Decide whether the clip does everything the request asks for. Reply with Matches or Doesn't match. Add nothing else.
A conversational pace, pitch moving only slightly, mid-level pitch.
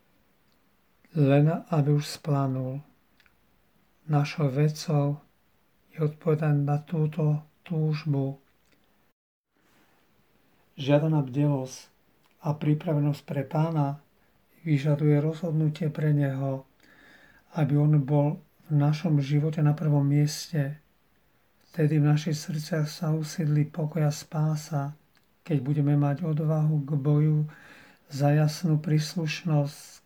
Doesn't match